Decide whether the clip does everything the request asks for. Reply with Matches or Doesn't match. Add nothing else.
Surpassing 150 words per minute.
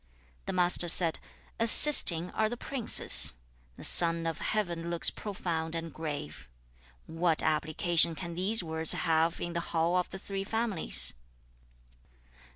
Doesn't match